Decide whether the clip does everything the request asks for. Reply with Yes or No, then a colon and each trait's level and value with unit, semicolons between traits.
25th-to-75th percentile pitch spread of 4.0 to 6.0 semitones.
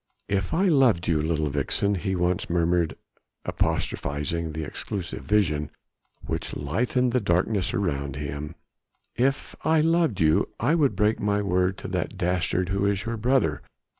Yes: wide, 5.5 semitones